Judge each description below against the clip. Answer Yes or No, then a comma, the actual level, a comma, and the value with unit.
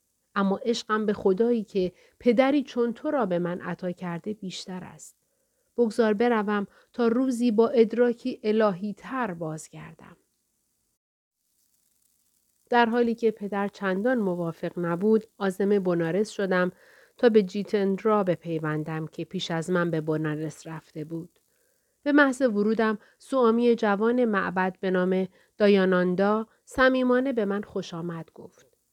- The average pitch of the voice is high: Yes, high, 205 Hz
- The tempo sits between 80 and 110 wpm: No, average, 130 wpm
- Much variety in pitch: No, average, 4.6 semitones